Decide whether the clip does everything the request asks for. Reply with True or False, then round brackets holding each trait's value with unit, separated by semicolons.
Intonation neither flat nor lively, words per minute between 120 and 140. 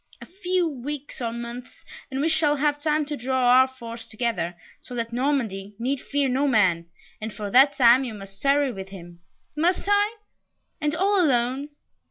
False (4.2 semitones; 180 wpm)